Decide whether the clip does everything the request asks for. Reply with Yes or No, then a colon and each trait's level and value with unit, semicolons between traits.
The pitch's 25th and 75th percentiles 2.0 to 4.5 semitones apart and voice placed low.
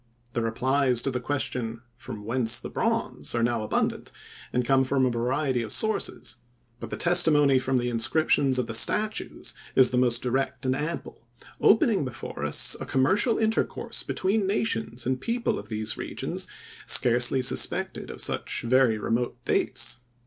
Yes: average, 3.6 semitones; low, 130 Hz